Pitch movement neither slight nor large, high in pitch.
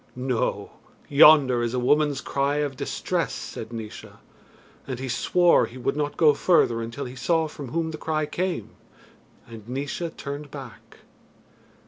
No: average, 3.5 semitones; medium, 140 Hz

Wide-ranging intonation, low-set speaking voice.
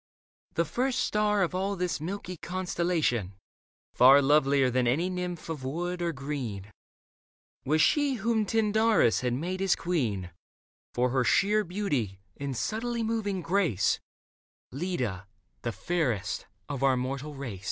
No: wide, 7.1 semitones; medium, 165 Hz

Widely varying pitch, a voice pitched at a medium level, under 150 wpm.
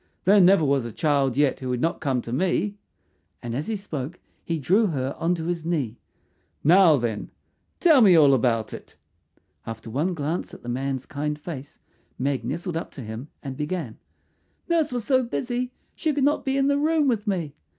No: wide, 7.2 semitones; medium, 160 Hz; average, 195 wpm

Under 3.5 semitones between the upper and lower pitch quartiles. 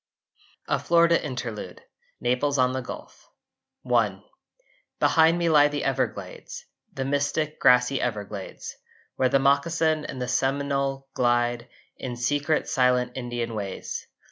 Yes: average, 3.0 semitones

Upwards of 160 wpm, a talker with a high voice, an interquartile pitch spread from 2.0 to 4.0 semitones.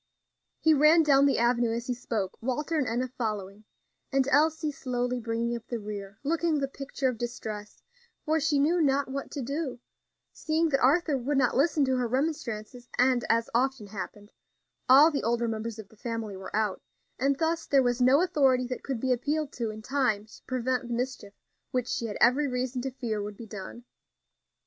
Yes: average, 195 wpm; very high, 250 Hz; average, 3.5 semitones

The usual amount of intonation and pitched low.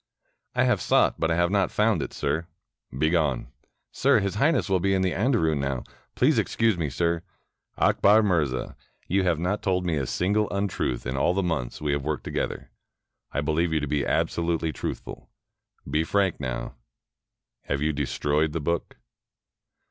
Yes: average, 4.5 semitones; very low, 85 Hz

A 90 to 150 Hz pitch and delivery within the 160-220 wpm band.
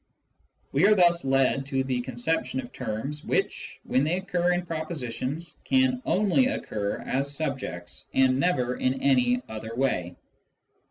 No: low, 135 Hz; average, 145 wpm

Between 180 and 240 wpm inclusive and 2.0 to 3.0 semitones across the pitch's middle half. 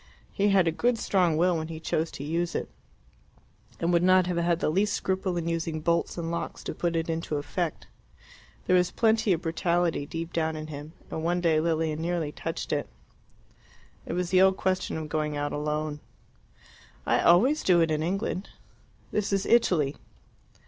Yes: average, 185 wpm; narrow, 2.5 semitones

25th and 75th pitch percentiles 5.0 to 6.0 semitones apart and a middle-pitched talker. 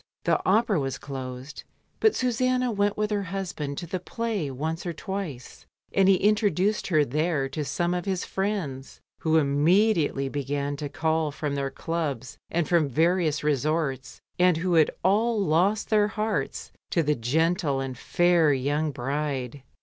Yes: average, 5.3 semitones; medium, 160 Hz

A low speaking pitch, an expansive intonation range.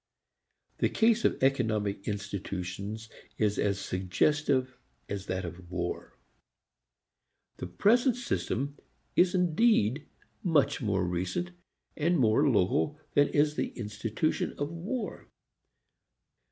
Yes: low, 120 Hz; wide, 7.7 semitones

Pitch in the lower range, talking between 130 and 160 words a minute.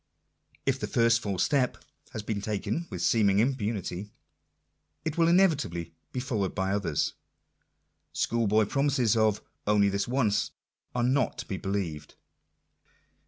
Yes: low, 110 Hz; slow, 135 wpm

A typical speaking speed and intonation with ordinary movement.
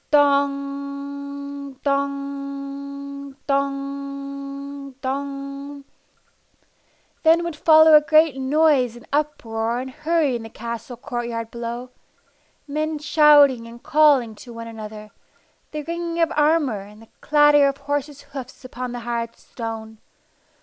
No: slow, 120 wpm; average, 3.0 semitones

